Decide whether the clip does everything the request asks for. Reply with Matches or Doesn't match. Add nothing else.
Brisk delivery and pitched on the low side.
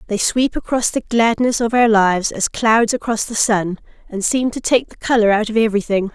Doesn't match